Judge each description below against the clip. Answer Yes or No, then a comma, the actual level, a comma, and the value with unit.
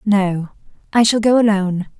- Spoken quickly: No, average, 150 wpm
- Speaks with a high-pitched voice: Yes, high, 205 Hz